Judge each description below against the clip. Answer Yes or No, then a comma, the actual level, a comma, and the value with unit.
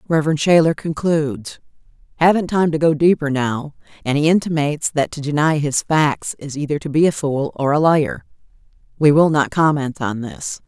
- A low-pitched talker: No, medium, 150 Hz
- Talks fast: No, average, 180 wpm